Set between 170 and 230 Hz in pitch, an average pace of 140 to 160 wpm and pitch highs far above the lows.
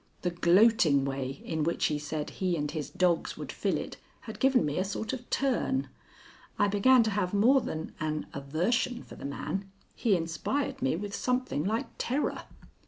No: medium, 185 Hz; average, 180 wpm; wide, 7.2 semitones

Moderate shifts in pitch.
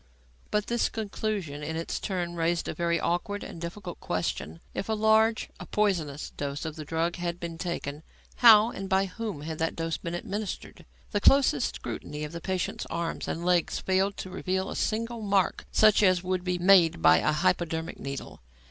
Yes: average, 3.7 semitones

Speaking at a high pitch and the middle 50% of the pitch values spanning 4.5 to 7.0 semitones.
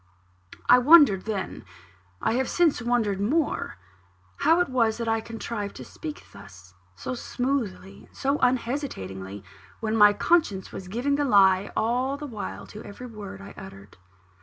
Yes: high, 225 Hz; average, 5.1 semitones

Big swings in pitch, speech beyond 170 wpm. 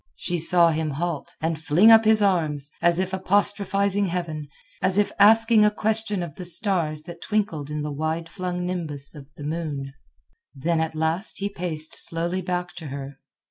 No: average, 4.1 semitones; average, 180 wpm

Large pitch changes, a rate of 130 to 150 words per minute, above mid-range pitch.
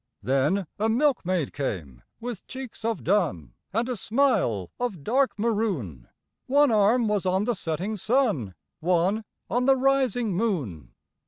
Yes: wide, 7.6 semitones; average, 140 wpm; high, 210 Hz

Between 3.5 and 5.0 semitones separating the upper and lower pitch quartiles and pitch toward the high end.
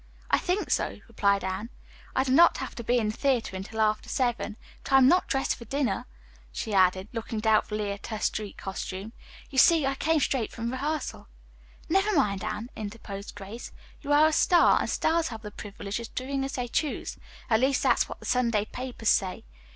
Yes: average, 4.5 semitones; high, 235 Hz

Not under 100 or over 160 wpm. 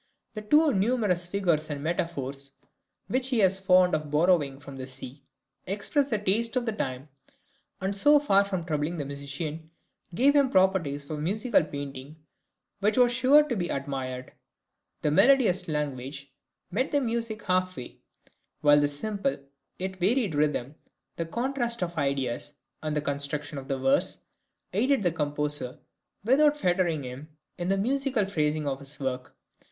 Yes: average, 155 wpm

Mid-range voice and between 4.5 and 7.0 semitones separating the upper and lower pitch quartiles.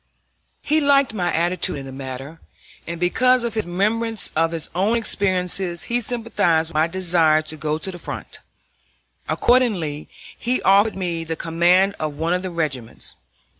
Yes: medium, 175 Hz; average, 5.0 semitones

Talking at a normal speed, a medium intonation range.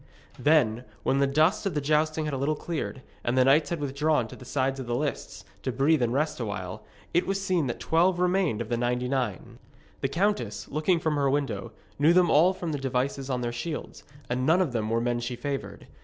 No: fast, 225 wpm; average, 4.3 semitones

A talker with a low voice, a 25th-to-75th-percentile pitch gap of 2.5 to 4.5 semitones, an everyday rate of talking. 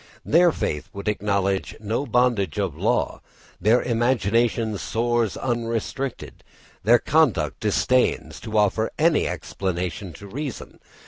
No: low, 115 Hz; average, 3.8 semitones; slow, 115 wpm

